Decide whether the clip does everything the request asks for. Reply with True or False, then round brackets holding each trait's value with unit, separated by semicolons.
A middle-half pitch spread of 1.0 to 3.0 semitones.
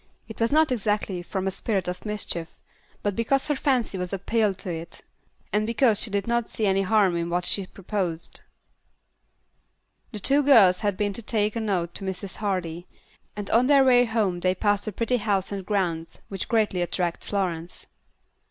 False (3.6 semitones)